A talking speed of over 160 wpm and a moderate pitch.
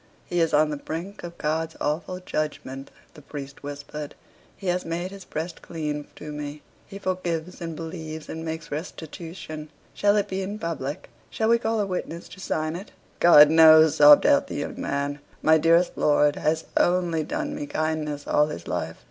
Yes: average, 180 wpm; medium, 160 Hz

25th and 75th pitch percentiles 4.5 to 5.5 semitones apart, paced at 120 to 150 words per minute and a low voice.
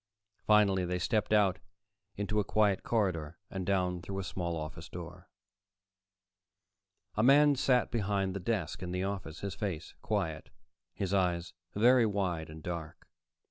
No: average, 3.2 semitones; average, 145 wpm; very low, 95 Hz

